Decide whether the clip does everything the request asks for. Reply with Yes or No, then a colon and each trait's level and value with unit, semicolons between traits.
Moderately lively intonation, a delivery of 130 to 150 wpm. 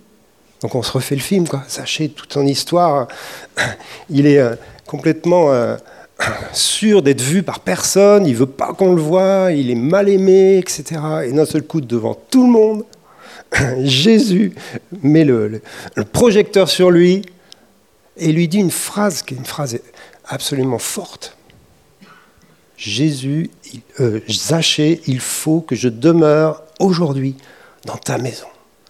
No: wide, 5.8 semitones; slow, 145 wpm